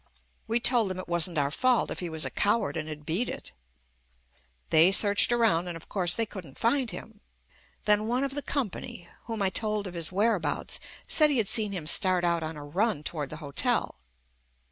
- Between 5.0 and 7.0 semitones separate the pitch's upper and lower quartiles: Yes, wide, 5.5 semitones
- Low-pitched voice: No, high, 190 Hz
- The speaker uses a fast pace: Yes, fast, 210 wpm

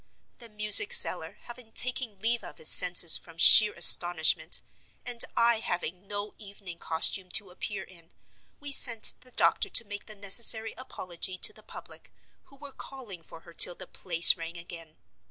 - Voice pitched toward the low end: No, high, 200 Hz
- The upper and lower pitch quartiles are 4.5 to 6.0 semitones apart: Yes, average, 5.0 semitones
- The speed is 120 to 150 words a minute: No, average, 170 wpm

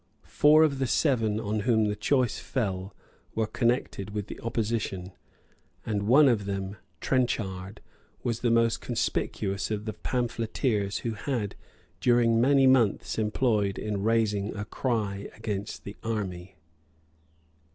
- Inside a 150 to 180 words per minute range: No, slow, 135 wpm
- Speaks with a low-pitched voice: Yes, low, 110 Hz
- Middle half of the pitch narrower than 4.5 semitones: Yes, average, 2.9 semitones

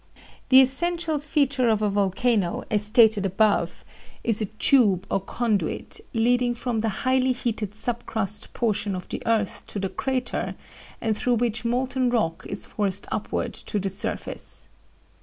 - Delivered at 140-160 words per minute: Yes, average, 155 wpm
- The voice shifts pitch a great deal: No, average, 3.4 semitones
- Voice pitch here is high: Yes, high, 225 Hz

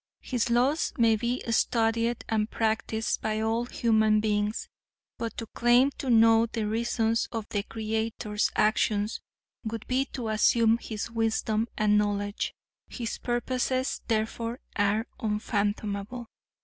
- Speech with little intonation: Yes, narrow, 1.7 semitones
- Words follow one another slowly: Yes, slow, 125 wpm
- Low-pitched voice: No, high, 225 Hz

